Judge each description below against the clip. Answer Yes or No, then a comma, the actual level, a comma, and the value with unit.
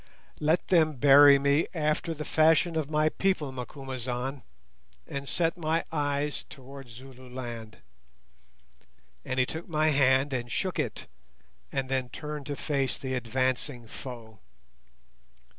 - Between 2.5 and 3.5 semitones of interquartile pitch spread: Yes, average, 3.0 semitones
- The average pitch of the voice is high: No, medium, 140 Hz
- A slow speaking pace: Yes, slow, 125 wpm